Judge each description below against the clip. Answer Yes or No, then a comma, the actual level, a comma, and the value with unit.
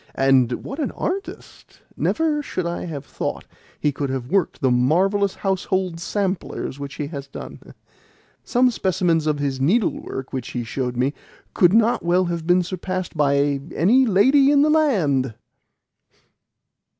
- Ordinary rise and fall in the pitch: No, wide, 6.4 semitones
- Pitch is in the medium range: Yes, medium, 170 Hz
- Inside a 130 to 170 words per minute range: Yes, average, 150 wpm